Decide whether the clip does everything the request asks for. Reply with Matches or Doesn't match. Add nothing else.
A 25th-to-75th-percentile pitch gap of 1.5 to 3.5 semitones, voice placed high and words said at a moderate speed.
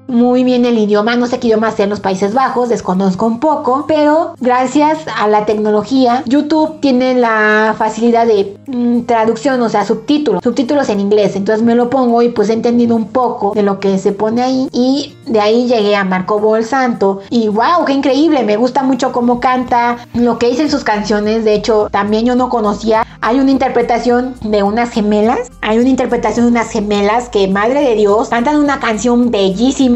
Doesn't match